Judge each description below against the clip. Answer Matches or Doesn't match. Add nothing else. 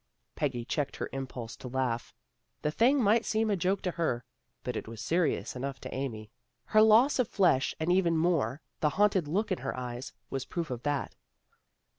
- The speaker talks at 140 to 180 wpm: Doesn't match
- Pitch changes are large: Matches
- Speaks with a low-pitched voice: Doesn't match